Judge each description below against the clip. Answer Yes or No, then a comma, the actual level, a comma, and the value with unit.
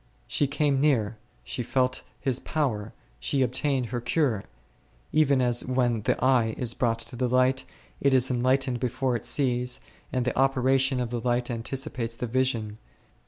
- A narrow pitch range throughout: Yes, narrow, 1.9 semitones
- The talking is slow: No, average, 165 wpm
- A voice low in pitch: Yes, low, 125 Hz